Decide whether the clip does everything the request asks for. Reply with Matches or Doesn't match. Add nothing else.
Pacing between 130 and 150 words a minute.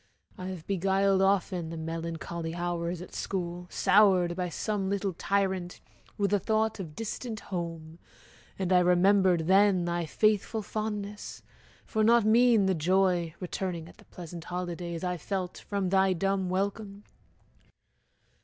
Matches